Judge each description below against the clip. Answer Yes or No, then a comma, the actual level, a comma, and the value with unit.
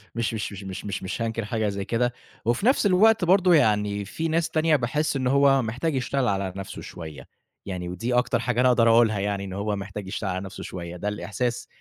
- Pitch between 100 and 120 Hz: Yes, low, 115 Hz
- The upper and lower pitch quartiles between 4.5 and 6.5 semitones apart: Yes, average, 4.9 semitones